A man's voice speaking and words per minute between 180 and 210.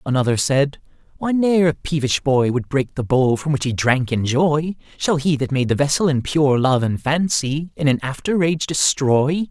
Yes: male; average, 200 wpm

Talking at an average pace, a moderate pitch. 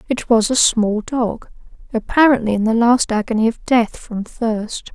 No: average, 170 wpm; high, 230 Hz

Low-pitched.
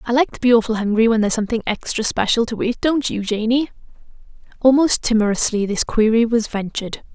No: high, 230 Hz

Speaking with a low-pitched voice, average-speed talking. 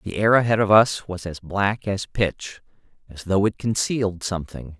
Yes: low, 100 Hz; average, 190 wpm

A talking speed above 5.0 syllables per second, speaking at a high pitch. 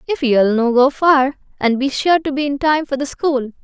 No: 4.8 syllables/s; very high, 275 Hz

